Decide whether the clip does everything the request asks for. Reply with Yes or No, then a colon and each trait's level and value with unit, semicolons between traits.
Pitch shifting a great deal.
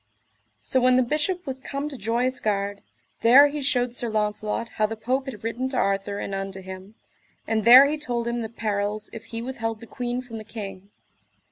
No: average, 3.4 semitones